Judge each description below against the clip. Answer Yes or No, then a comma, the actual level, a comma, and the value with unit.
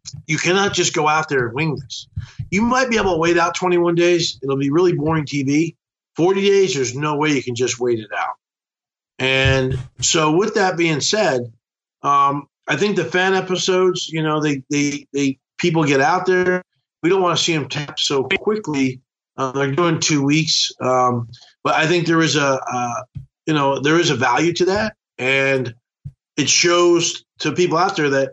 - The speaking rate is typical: Yes, average, 190 wpm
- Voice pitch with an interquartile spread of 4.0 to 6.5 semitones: Yes, average, 4.4 semitones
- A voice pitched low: No, medium, 150 Hz